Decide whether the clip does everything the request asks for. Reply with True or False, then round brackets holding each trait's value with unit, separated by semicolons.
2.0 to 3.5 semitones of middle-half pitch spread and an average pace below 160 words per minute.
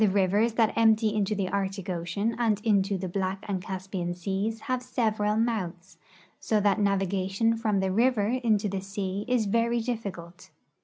False (2.8 semitones; 165 wpm)